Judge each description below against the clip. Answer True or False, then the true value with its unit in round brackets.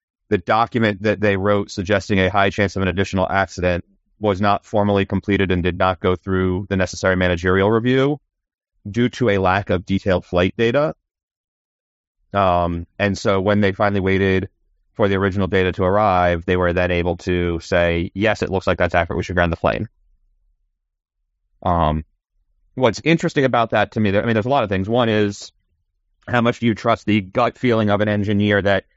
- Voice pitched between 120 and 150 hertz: False (95 Hz)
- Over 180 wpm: True (190 wpm)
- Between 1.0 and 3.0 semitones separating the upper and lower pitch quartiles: True (2.7 semitones)